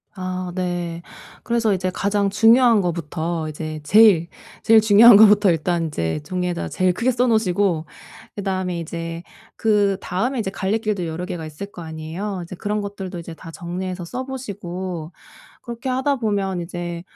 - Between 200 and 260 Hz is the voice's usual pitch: No, medium, 185 Hz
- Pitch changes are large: No, average, 3.6 semitones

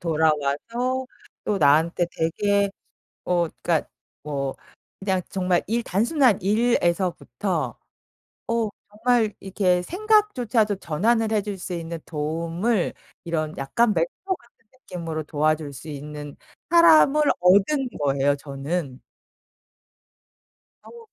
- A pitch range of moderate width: No, wide, 6.5 semitones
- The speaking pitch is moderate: Yes, medium, 180 Hz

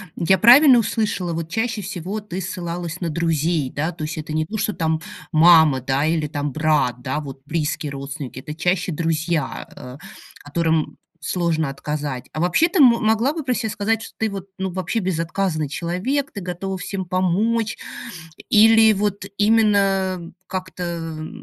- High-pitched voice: No, medium, 175 Hz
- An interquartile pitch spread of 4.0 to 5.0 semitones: Yes, average, 4.7 semitones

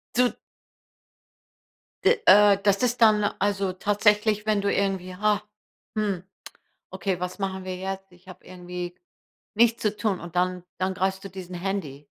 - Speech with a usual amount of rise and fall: No, narrow, 2.2 semitones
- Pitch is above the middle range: Yes, high, 195 Hz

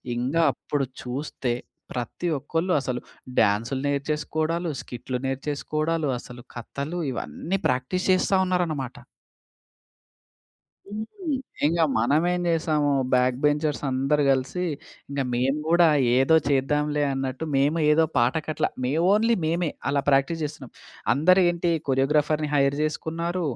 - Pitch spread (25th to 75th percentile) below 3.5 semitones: No, average, 3.8 semitones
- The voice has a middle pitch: Yes, medium, 150 Hz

